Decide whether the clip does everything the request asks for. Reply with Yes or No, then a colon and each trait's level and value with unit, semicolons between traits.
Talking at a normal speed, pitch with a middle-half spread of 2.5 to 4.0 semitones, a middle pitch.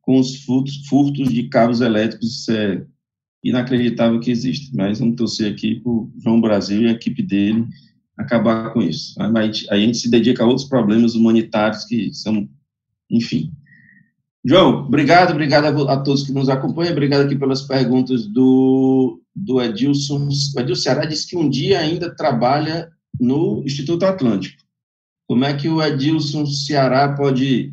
No: average, 160 wpm; average, 3.7 semitones; low, 130 Hz